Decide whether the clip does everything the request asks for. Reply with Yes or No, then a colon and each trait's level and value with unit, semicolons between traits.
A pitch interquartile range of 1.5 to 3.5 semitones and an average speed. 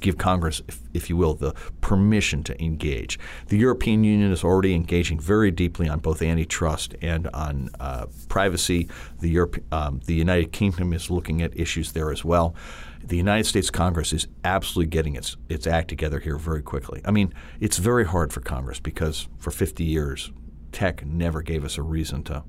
Yes: average, 2.9 semitones; average, 185 wpm